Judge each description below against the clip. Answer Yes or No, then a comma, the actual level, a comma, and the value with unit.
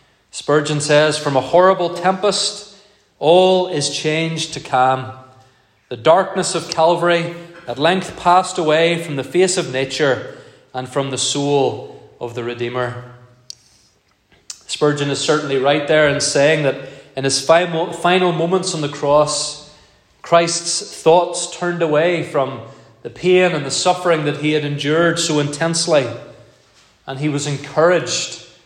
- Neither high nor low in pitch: Yes, medium, 150 Hz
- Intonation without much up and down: No, average, 4.1 semitones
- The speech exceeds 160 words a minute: No, average, 140 wpm